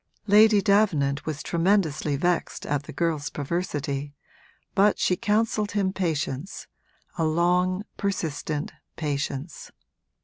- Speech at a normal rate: No, slow, 105 wpm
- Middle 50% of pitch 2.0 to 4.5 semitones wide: No, average, 5.2 semitones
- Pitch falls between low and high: Yes, medium, 170 Hz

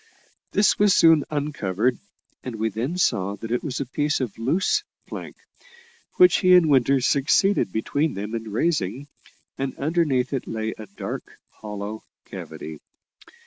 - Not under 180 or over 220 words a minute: No, average, 145 wpm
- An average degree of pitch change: No, wide, 5.8 semitones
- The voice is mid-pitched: No, low, 130 Hz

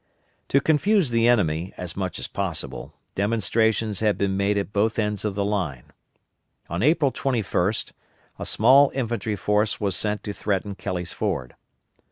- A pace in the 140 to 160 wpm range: Yes, average, 155 wpm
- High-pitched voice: No, low, 105 Hz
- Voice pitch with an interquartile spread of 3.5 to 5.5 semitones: No, average, 3.0 semitones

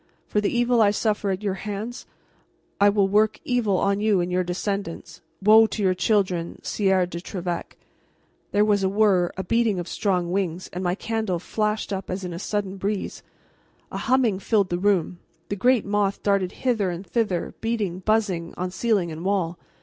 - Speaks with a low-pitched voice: No, high, 195 Hz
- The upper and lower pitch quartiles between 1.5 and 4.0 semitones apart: Yes, average, 2.8 semitones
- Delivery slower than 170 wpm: No, average, 185 wpm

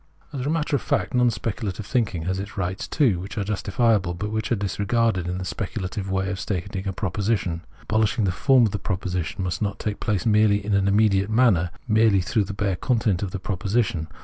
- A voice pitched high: No, low, 100 Hz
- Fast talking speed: Yes, fast, 210 wpm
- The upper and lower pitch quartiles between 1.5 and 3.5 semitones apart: Yes, average, 2.8 semitones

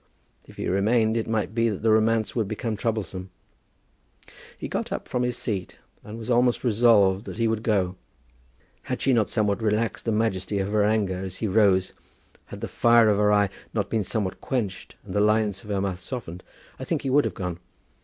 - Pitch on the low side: Yes, low, 105 Hz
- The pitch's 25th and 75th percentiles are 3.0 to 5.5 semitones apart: No, narrow, 2.6 semitones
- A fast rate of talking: Yes, fast, 210 wpm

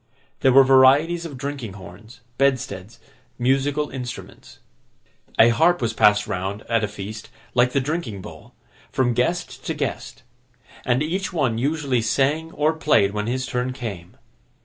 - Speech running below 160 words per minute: Yes, average, 150 wpm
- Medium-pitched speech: No, low, 125 Hz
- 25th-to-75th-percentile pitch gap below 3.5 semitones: No, average, 4.7 semitones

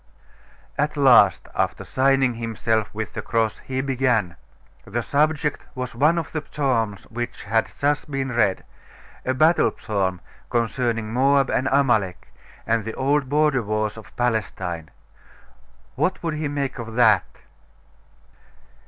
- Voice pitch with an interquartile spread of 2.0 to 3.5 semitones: No, average, 4.1 semitones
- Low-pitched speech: Yes, low, 125 Hz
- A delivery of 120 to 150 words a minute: Yes, slow, 135 wpm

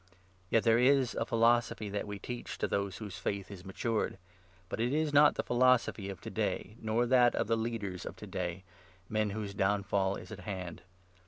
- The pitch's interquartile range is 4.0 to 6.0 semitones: No, average, 3.2 semitones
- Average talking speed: No, fast, 210 wpm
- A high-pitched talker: No, low, 110 Hz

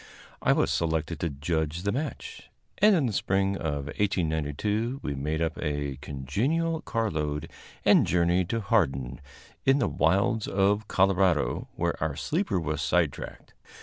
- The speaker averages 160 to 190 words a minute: No, average, 145 wpm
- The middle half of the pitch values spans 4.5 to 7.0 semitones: Yes, wide, 5.6 semitones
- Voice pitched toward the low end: Yes, very low, 85 Hz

